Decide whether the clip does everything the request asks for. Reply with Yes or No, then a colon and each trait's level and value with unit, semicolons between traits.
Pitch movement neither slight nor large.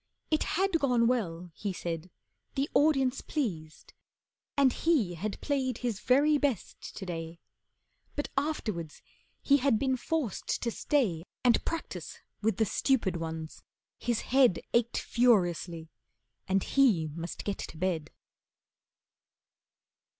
No: wide, 7.8 semitones